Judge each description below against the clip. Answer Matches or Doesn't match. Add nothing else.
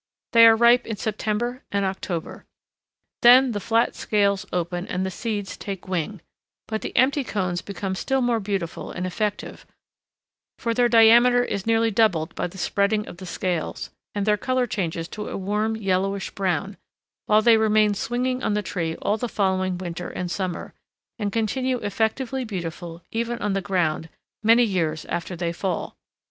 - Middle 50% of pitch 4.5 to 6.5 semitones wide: Doesn't match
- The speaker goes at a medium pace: Matches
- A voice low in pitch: Doesn't match